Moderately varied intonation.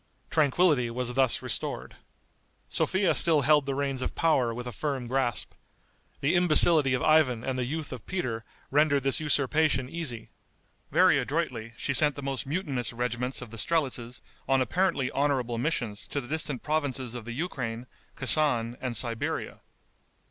Yes: average, 3.8 semitones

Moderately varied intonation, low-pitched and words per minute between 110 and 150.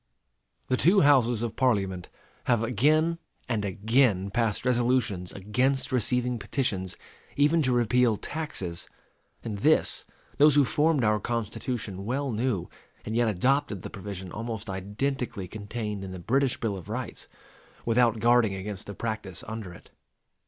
Yes: average, 4.0 semitones; low, 115 Hz; average, 140 wpm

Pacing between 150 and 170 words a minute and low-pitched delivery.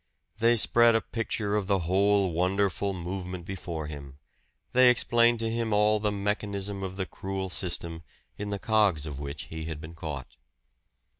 Yes: average, 165 wpm; very low, 95 Hz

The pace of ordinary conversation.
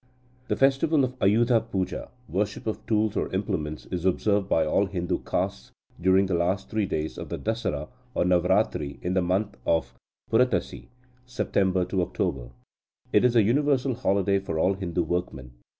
Yes: average, 160 wpm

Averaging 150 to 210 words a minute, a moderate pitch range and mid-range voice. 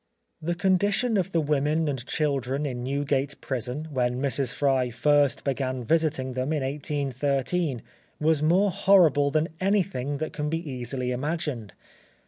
No: average, 140 wpm; average, 3.4 semitones; medium, 145 Hz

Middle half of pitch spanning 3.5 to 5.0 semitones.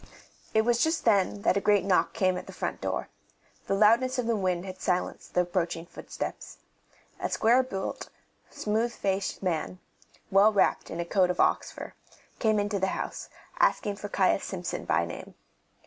No: average, 2.9 semitones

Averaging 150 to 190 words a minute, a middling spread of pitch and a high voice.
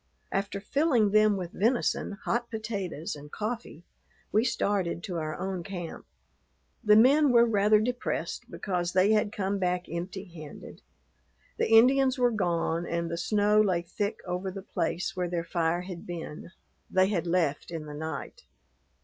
Yes: average, 160 wpm; average, 3.9 semitones; high, 195 Hz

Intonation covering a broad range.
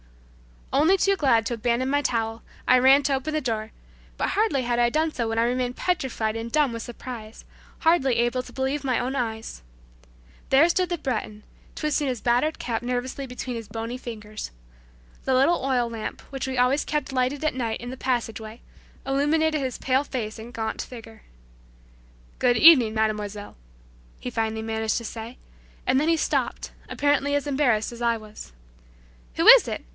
No: average, 3.4 semitones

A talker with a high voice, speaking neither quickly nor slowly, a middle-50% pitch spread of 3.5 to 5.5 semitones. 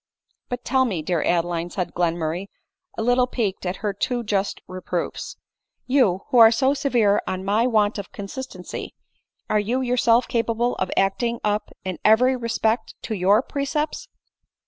Yes: high, 220 Hz; average, 165 wpm; average, 4.7 semitones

